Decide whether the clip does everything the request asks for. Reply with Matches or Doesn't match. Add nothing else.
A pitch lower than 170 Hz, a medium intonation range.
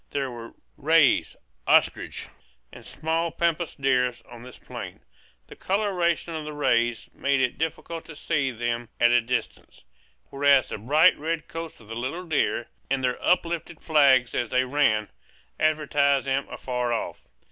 Matches